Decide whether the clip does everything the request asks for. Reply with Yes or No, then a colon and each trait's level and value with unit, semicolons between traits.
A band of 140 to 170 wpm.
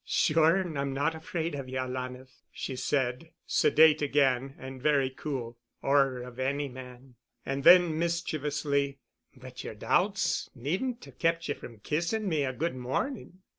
Yes: average, 155 wpm